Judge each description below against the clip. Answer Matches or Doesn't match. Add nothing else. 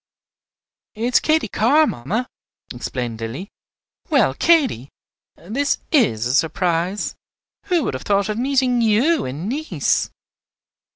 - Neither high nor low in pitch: Doesn't match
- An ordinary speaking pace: Doesn't match